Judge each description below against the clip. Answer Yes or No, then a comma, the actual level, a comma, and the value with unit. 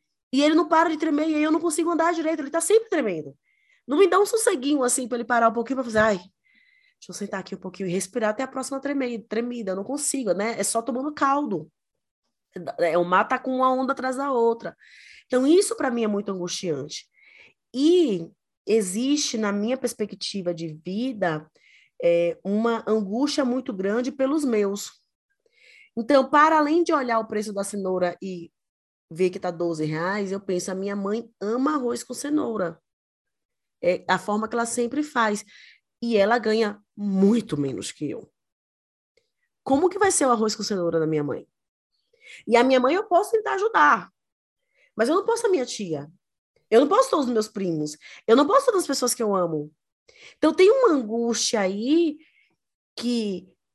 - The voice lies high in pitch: Yes, high, 240 Hz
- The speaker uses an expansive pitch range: Yes, wide, 7.4 semitones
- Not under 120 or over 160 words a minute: No, fast, 185 wpm